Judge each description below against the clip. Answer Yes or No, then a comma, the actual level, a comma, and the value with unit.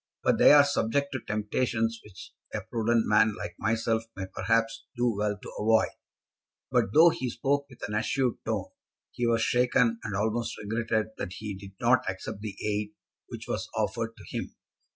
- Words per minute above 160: Yes, average, 175 wpm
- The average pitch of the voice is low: Yes, low, 115 Hz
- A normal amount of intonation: No, narrow, 2.3 semitones